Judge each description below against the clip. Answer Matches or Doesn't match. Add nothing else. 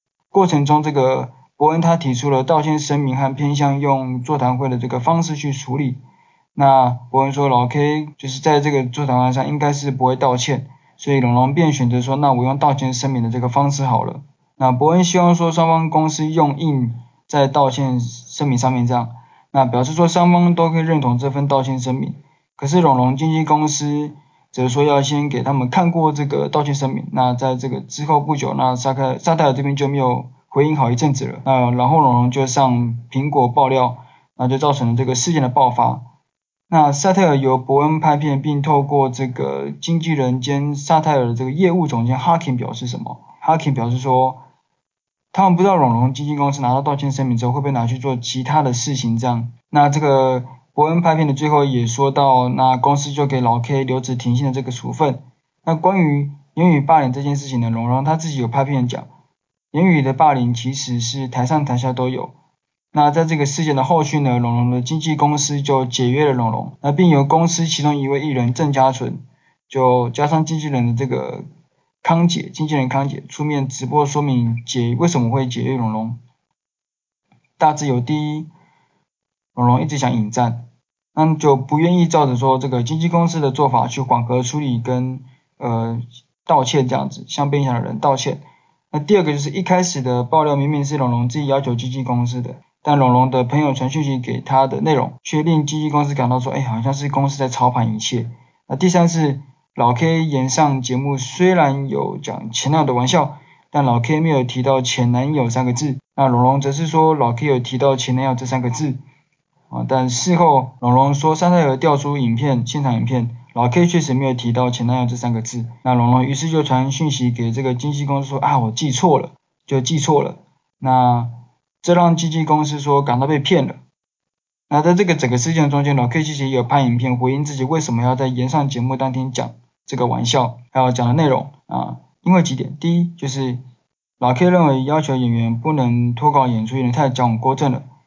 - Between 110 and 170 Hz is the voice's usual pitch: Matches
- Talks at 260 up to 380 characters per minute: Matches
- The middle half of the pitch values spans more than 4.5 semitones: Doesn't match